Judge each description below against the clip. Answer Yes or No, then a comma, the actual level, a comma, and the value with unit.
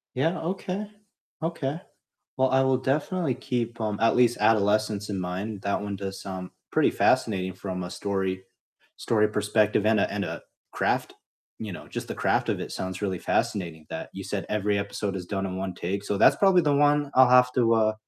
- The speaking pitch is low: Yes, low, 105 Hz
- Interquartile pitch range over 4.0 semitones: Yes, average, 4.7 semitones